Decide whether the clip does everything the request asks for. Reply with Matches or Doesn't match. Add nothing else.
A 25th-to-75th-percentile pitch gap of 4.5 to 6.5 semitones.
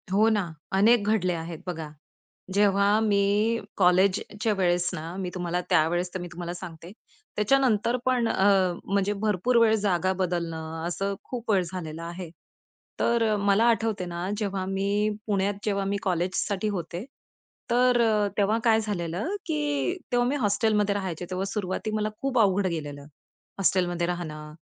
Doesn't match